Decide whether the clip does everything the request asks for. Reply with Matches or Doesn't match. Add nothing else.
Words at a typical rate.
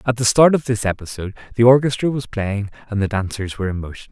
Doesn't match